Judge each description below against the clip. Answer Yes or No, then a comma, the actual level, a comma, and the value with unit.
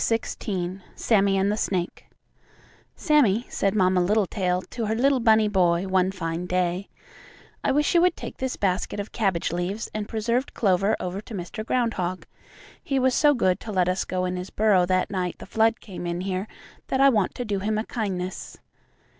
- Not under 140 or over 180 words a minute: No, average, 190 wpm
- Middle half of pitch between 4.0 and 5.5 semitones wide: No, average, 3.5 semitones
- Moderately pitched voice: No, high, 195 Hz